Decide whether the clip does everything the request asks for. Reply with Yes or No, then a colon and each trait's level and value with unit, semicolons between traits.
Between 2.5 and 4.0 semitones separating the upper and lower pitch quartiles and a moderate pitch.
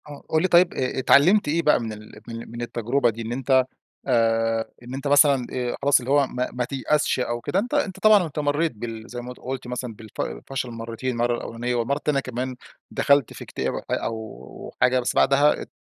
No: average, 3.5 semitones; low, 125 Hz